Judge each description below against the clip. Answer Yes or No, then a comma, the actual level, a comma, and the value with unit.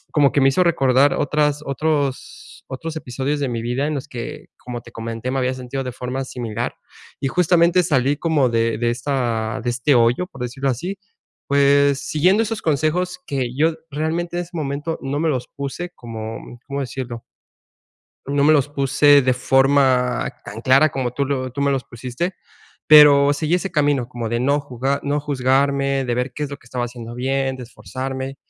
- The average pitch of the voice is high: No, low, 135 Hz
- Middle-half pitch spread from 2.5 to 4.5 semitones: Yes, average, 2.8 semitones